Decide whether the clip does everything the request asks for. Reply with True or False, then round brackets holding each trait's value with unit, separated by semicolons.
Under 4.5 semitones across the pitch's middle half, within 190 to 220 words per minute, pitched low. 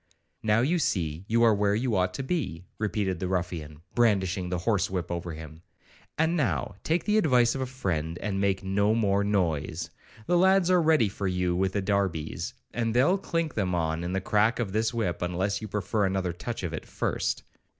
False (4.8 semitones; 200 wpm; 100 Hz)